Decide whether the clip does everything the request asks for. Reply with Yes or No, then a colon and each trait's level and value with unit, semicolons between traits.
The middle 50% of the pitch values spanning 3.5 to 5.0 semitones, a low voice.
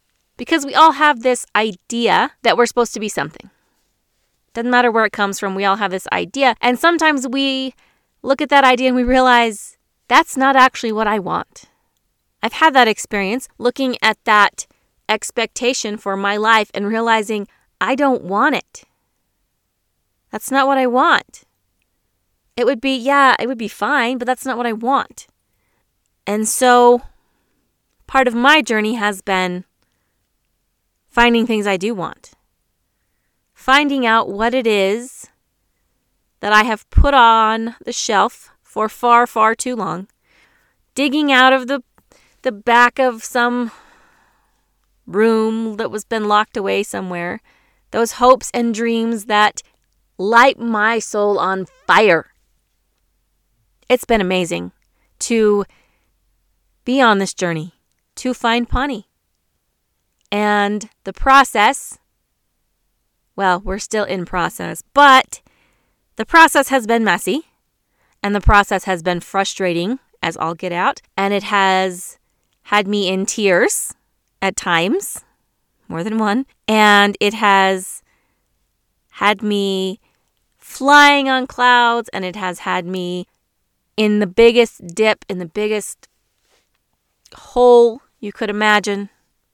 No: average, 4.0 semitones; high, 220 Hz